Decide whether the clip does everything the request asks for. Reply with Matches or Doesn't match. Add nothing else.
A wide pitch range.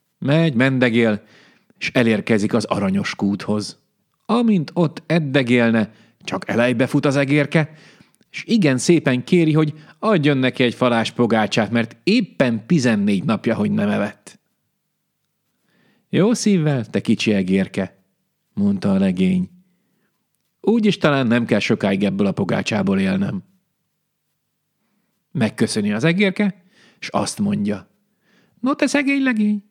Matches